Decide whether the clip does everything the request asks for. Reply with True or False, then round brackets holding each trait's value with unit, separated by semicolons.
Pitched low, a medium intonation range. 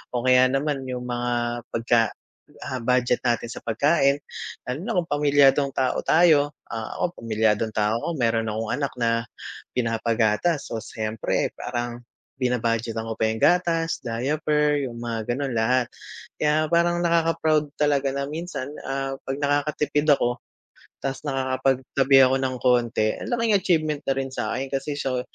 True (130 Hz; 3.8 semitones)